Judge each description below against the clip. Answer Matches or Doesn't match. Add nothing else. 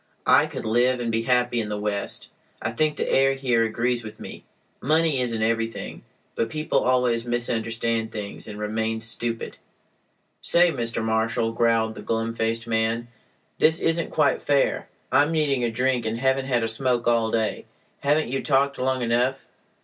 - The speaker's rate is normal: Matches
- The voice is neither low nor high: Doesn't match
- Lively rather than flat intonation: Doesn't match